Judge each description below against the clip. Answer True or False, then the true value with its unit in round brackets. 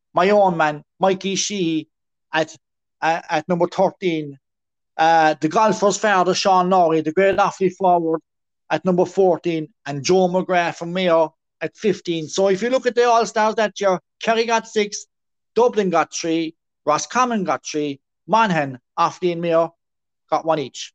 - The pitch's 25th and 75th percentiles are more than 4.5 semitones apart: False (3.6 semitones)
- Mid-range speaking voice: True (175 Hz)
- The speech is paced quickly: False (160 wpm)